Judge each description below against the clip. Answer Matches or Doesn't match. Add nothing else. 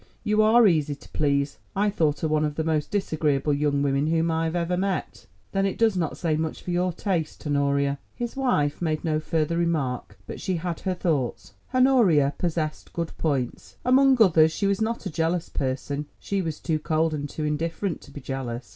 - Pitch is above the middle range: Doesn't match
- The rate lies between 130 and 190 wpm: Doesn't match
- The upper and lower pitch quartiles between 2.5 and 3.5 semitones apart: Doesn't match